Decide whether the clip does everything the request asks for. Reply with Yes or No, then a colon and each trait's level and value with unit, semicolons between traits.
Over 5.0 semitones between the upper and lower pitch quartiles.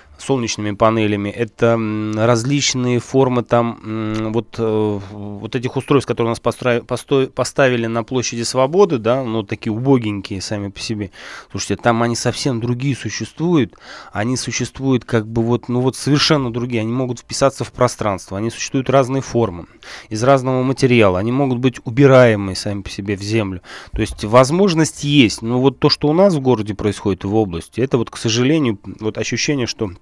No: average, 3.3 semitones